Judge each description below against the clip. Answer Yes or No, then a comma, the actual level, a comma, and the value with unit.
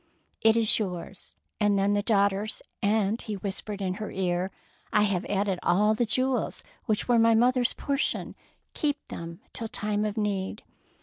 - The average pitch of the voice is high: Yes, high, 210 Hz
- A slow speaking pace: No, average, 175 wpm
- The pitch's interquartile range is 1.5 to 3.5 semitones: Yes, narrow, 2.4 semitones